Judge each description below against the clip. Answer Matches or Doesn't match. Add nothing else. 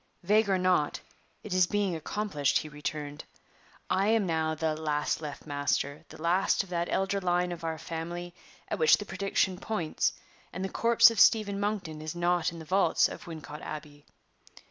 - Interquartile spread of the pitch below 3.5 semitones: Doesn't match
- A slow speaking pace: Doesn't match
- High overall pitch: Doesn't match